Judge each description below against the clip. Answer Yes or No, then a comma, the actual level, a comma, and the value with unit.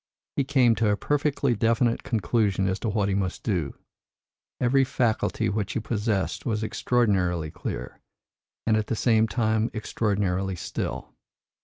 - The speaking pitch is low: Yes, low, 110 Hz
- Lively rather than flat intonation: No, average, 3.1 semitones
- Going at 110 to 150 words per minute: Yes, average, 145 wpm